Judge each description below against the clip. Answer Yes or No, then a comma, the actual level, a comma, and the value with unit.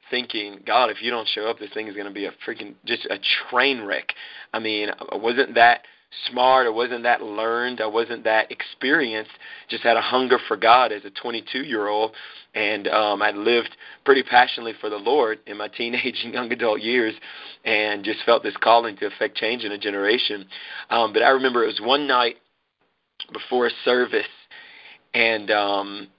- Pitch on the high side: No, low, 115 Hz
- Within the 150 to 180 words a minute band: No, average, 190 wpm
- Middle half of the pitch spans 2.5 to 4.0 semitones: Yes, average, 2.9 semitones